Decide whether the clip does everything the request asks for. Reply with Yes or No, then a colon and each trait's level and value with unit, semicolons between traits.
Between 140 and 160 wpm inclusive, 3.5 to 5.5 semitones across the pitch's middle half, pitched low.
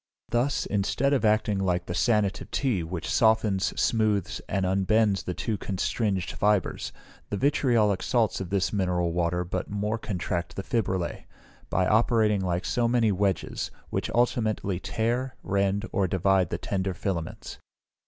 No: average, 145 wpm; average, 3.1 semitones; low, 100 Hz